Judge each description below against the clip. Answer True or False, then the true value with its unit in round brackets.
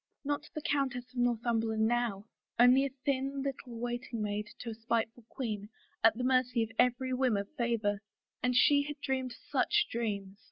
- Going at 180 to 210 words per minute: True (185 wpm)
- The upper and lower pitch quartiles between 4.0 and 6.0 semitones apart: False (2.7 semitones)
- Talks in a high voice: True (245 Hz)